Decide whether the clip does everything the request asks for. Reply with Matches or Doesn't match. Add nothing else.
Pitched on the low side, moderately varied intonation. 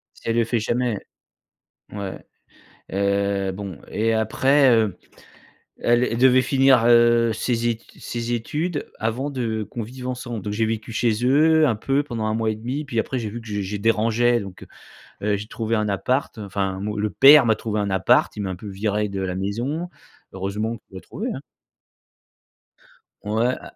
Matches